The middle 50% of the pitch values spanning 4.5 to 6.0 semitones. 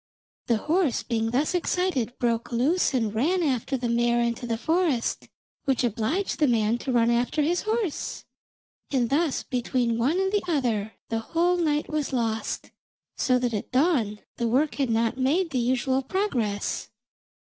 Yes: average, 5.2 semitones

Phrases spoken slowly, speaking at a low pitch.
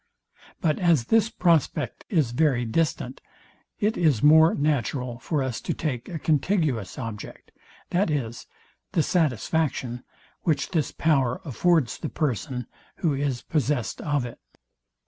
No: slow, 125 wpm; medium, 145 Hz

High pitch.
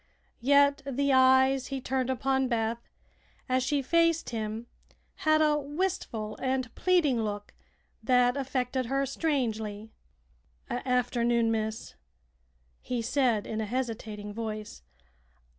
Yes: very high, 255 Hz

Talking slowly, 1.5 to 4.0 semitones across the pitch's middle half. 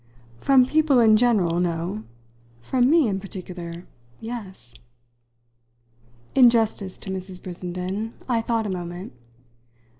No: slow, 115 wpm; average, 4.7 semitones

